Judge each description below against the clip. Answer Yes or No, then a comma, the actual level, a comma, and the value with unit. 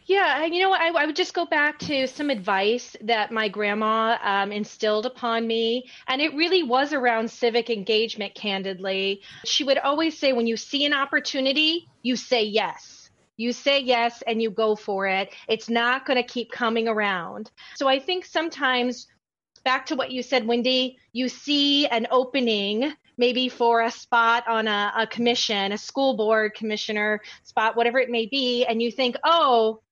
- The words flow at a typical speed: Yes, average, 180 wpm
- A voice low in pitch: No, high, 240 Hz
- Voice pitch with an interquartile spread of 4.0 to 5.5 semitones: No, average, 3.6 semitones